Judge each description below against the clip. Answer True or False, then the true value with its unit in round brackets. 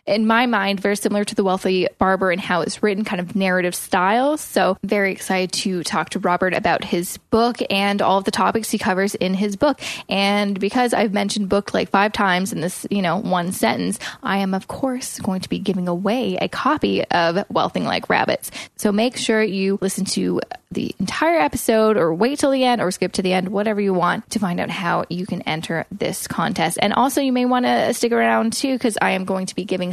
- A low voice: False (200 Hz)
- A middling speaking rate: False (225 wpm)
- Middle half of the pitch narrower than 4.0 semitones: True (3.1 semitones)